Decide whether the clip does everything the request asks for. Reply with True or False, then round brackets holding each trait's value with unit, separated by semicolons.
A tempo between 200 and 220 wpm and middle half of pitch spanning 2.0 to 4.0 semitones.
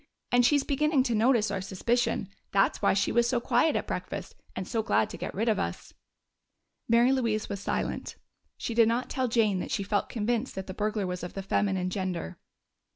True (205 wpm; 3.7 semitones)